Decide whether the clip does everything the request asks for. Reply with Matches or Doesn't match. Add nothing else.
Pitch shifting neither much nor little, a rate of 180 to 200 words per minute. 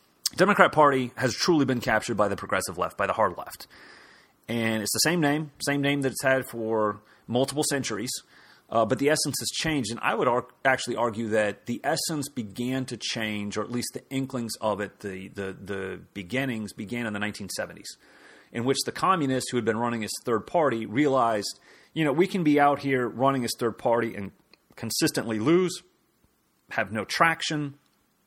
Matches